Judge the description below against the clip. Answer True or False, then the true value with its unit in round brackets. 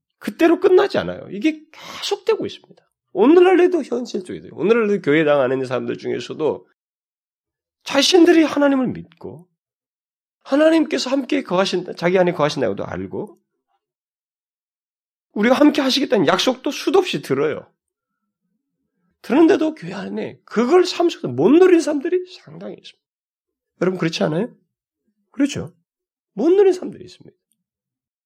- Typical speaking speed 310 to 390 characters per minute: True (320 characters per minute)